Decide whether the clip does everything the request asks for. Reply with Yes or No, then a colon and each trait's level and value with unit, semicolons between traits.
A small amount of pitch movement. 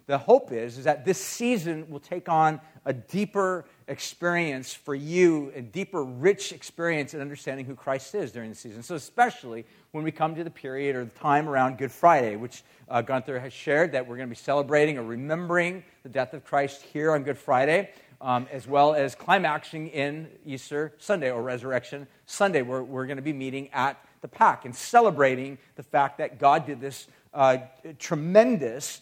No: average, 3.3 semitones